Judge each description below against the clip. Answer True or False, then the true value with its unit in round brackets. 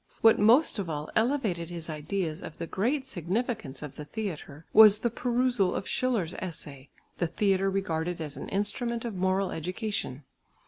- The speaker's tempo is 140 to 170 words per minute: True (165 wpm)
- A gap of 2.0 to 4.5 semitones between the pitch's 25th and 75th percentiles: False (5.5 semitones)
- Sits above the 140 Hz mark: True (190 Hz)